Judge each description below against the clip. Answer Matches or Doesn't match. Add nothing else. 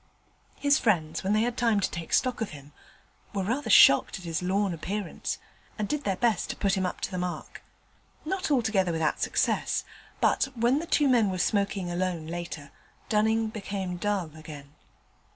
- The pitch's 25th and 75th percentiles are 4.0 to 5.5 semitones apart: Matches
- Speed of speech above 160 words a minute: Matches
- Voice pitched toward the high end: Matches